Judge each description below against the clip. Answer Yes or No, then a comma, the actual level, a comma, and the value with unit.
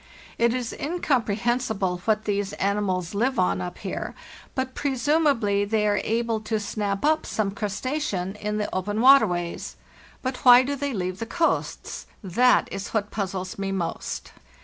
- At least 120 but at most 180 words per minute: Yes, average, 150 wpm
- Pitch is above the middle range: Yes, high, 215 Hz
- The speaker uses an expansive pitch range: No, average, 4.3 semitones